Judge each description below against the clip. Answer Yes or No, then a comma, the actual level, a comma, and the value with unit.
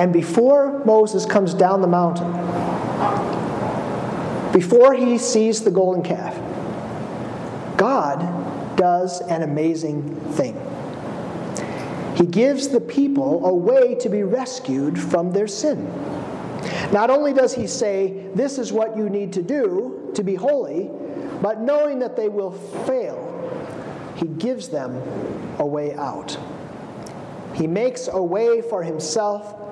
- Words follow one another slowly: Yes, slow, 125 wpm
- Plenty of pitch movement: Yes, wide, 6.5 semitones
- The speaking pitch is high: Yes, high, 210 Hz